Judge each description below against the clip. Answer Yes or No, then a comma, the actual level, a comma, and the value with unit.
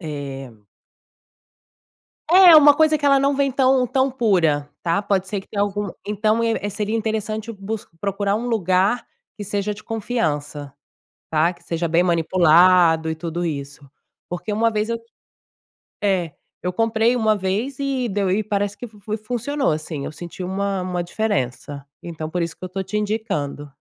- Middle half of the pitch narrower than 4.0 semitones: No, average, 4.8 semitones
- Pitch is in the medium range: No, high, 200 Hz